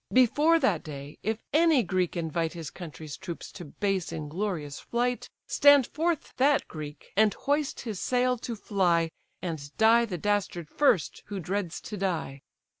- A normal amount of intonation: No, wide, 7.0 semitones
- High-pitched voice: Yes, high, 195 Hz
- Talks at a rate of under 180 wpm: Yes, average, 155 wpm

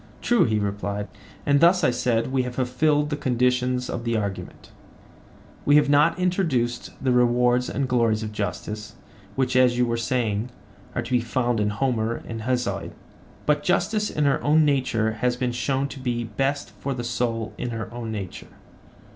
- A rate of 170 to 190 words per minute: Yes, average, 180 wpm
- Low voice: Yes, low, 125 Hz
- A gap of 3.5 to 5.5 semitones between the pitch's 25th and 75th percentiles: No, average, 3.0 semitones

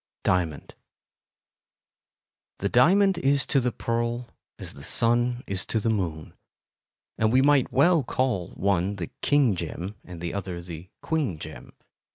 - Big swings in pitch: Yes, wide, 6.6 semitones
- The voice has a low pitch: Yes, low, 110 Hz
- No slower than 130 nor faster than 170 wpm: Yes, average, 145 wpm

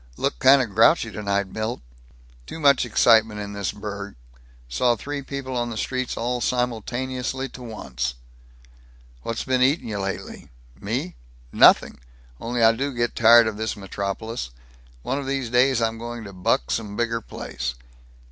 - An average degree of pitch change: Yes, average, 3.5 semitones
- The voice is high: No, low, 115 Hz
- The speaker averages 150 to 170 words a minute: Yes, average, 155 wpm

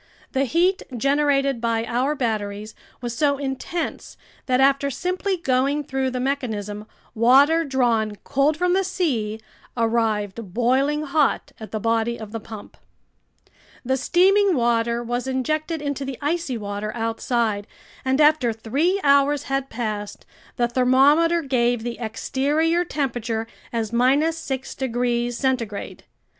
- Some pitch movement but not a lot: Yes, average, 4.0 semitones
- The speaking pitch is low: No, very high, 260 Hz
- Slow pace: Yes, slow, 130 wpm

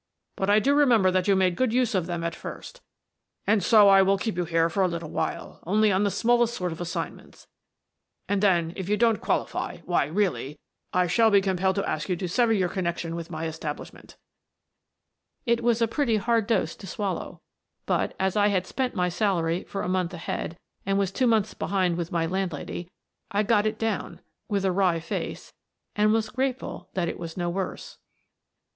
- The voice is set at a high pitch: Yes, high, 195 Hz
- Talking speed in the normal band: No, fast, 215 wpm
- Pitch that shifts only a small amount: No, average, 3.8 semitones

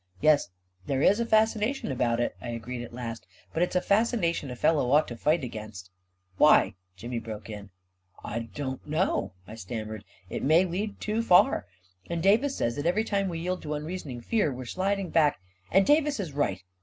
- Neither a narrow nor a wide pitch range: No, wide, 8.4 semitones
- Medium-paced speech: No, fast, 210 wpm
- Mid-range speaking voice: Yes, medium, 150 Hz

